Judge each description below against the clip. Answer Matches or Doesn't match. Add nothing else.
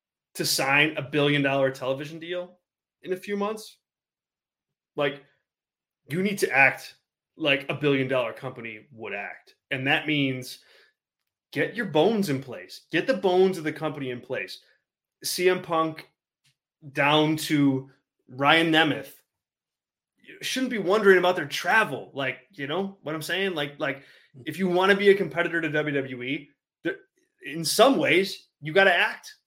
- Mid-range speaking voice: Matches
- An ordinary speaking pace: Matches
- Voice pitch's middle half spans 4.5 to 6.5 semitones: Matches